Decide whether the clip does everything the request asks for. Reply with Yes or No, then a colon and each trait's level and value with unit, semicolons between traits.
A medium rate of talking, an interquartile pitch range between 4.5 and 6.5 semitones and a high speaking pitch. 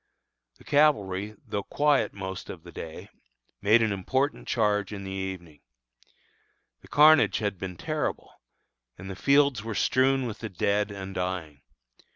No: average, 150 wpm; average, 5.3 semitones; low, 100 Hz